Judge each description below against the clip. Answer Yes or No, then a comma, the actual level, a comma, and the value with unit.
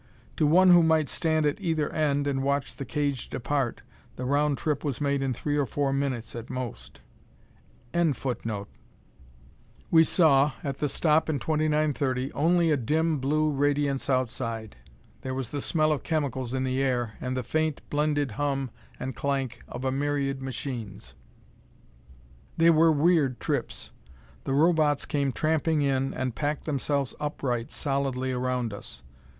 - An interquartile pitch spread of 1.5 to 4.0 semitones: Yes, narrow, 2.6 semitones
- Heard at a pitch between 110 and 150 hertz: Yes, medium, 140 Hz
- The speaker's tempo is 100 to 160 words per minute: Yes, average, 150 wpm